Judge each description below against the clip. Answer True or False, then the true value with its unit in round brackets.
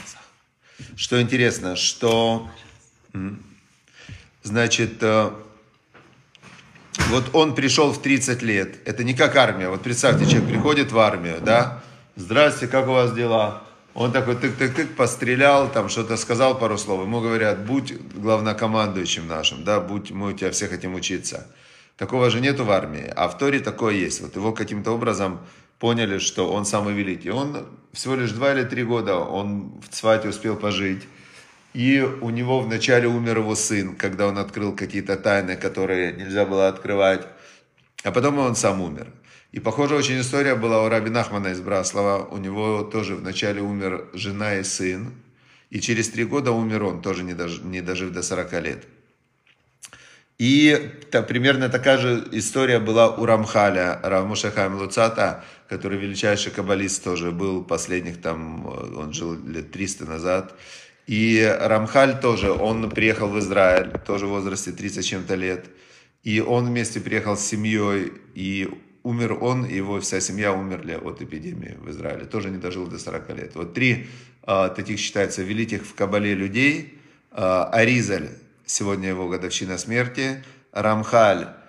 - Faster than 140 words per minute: True (150 wpm)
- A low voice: True (105 Hz)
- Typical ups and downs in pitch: True (3.8 semitones)